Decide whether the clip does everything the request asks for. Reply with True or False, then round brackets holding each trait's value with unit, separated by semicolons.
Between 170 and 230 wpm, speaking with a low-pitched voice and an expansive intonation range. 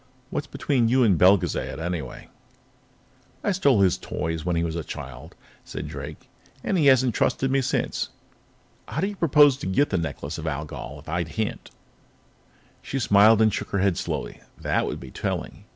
True (180 wpm; 100 Hz; 8.2 semitones)